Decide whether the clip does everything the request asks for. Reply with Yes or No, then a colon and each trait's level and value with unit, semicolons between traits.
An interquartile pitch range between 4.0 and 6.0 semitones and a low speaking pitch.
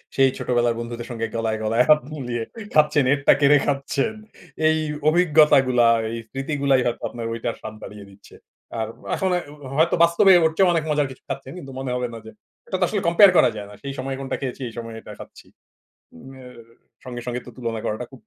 Yes: average, 4.3 semitones; low, 130 Hz